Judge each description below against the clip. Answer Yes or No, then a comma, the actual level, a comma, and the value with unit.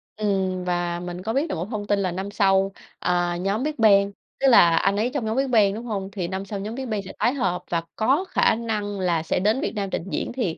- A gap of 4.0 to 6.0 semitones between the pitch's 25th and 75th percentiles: No, average, 3.4 semitones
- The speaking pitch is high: Yes, high, 200 Hz